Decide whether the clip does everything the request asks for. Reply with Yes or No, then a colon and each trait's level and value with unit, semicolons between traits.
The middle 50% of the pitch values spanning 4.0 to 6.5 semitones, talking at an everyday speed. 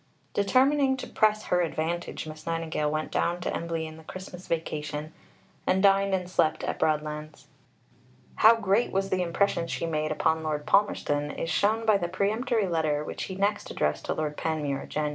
Yes: average, 4.3 semitones; average, 180 wpm